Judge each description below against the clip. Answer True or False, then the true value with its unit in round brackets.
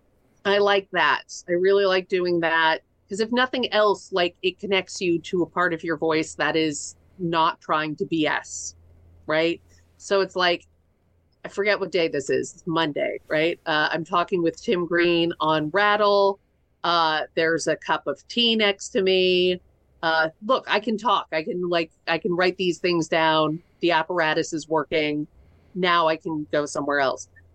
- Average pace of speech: True (180 wpm)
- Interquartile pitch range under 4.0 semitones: True (3.2 semitones)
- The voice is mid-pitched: True (170 Hz)